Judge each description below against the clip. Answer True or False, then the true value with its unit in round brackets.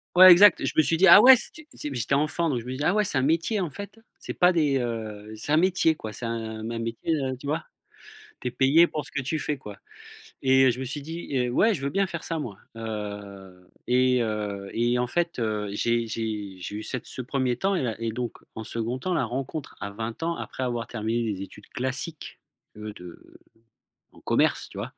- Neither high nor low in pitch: False (125 Hz)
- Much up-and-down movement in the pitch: True (6.0 semitones)